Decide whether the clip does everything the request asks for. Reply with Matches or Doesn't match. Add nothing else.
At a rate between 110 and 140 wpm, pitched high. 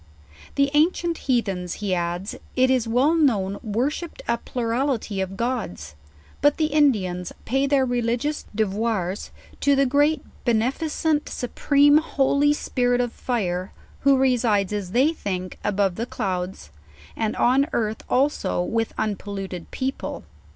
Matches